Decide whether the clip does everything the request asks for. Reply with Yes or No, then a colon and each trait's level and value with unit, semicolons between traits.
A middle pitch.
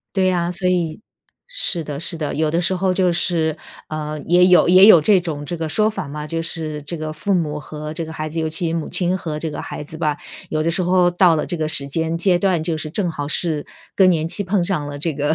Yes: medium, 165 Hz